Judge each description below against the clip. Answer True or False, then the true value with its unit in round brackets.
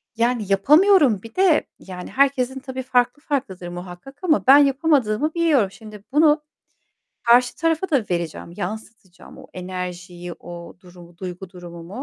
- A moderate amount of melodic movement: False (7.5 semitones)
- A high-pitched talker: True (225 Hz)